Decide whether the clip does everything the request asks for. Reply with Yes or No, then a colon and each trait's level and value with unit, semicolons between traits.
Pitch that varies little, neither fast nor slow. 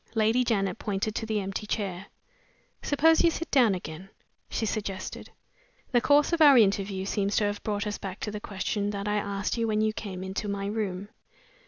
Yes: narrow, 2.2 semitones; average, 195 wpm